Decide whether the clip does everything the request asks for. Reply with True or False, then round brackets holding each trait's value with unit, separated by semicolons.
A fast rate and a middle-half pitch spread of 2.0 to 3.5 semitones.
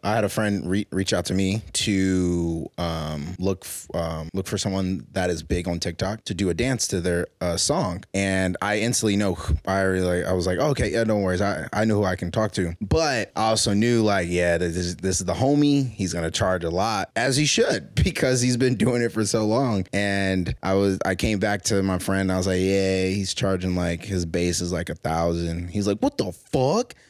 True (240 wpm; 2.9 semitones)